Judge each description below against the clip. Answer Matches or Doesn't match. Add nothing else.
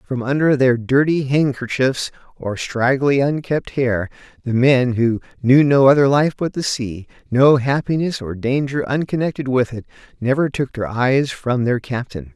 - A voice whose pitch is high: Doesn't match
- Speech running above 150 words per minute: Matches